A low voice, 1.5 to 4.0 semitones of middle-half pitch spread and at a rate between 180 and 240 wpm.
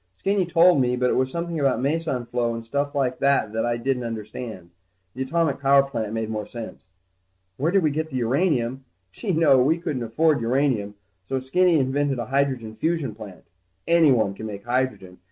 No: low, 130 Hz; average, 4.5 semitones; average, 190 wpm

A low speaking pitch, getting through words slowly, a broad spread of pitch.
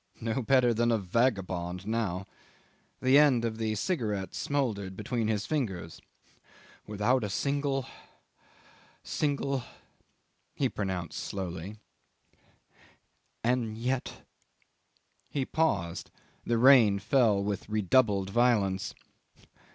No: low, 110 Hz; slow, 100 wpm; average, 4.5 semitones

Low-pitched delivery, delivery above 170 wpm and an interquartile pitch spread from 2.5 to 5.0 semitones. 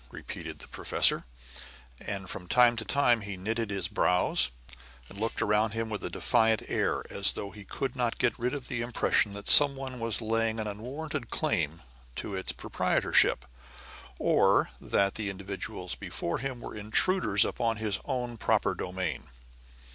No: low, 110 Hz; average, 160 wpm; average, 3.5 semitones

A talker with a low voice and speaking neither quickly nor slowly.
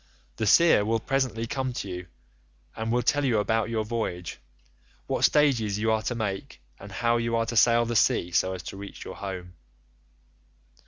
Yes: low, 110 Hz; average, 180 wpm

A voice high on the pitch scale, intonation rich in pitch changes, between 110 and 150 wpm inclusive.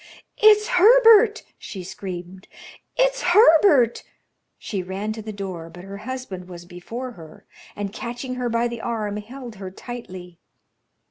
Yes: high, 220 Hz; wide, 5.7 semitones; average, 140 wpm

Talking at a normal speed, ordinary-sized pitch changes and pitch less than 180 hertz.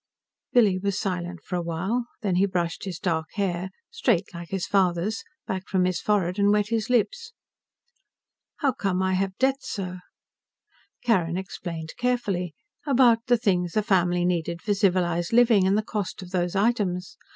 No: average, 165 wpm; average, 3.4 semitones; high, 190 Hz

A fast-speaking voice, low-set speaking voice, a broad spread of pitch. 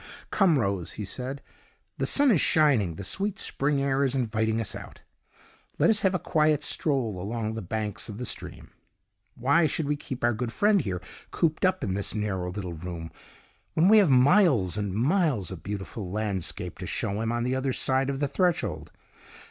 No: average, 190 wpm; low, 125 Hz; wide, 6.8 semitones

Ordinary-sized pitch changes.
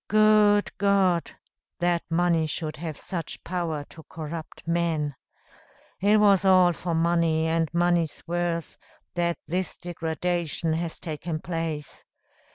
No: narrow, 1.7 semitones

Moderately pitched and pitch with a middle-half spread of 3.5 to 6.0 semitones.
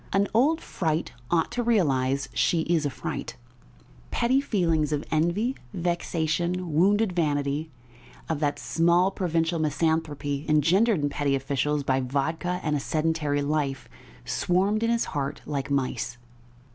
Yes: medium, 160 Hz; average, 3.8 semitones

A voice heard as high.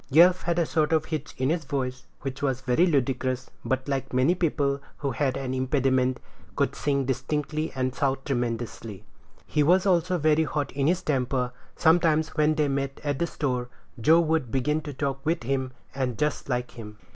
No: medium, 140 Hz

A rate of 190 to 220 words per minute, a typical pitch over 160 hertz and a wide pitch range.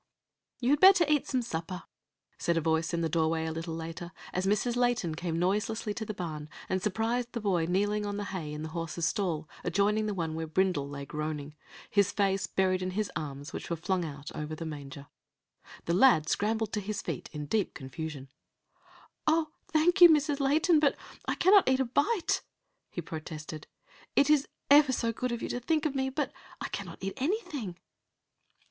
Yes: average, 195 wpm; high, 190 Hz; wide, 7.3 semitones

